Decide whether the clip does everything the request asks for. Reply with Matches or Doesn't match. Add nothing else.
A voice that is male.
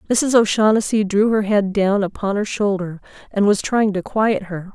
Doesn't match